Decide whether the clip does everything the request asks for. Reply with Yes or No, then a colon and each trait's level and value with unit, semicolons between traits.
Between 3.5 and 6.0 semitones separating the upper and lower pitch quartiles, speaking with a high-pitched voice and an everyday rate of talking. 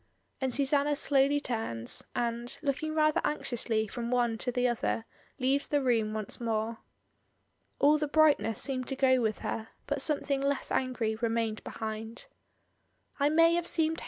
Yes: average, 4.1 semitones; very high, 255 Hz; average, 160 wpm